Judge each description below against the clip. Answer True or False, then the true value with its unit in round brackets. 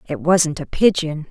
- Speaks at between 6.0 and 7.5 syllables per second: False (4.5 syllables/s)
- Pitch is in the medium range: True (165 Hz)